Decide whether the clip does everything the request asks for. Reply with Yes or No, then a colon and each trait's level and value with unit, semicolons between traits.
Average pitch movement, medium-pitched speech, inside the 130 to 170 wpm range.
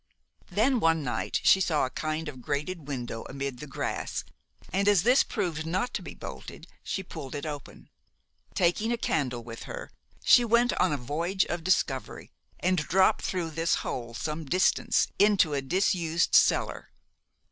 Yes: average, 5.0 semitones; medium, 165 Hz; average, 165 wpm